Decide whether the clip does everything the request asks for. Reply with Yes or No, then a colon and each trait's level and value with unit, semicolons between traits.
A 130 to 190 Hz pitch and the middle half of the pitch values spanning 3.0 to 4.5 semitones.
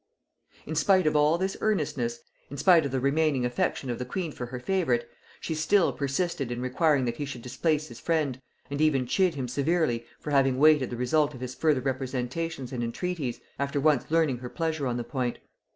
Yes: medium, 140 Hz; average, 4.0 semitones